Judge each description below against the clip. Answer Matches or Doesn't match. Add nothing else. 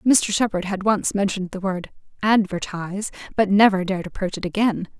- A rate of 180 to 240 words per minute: Doesn't match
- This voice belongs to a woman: Matches